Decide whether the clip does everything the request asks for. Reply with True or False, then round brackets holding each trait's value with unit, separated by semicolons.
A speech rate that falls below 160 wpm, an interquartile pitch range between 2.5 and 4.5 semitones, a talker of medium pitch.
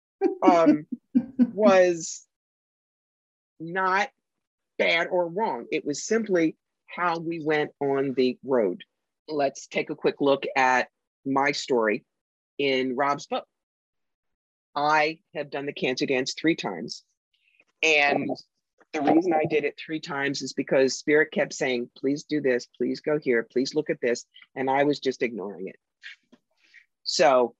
True (140 wpm; 4.2 semitones; 150 Hz)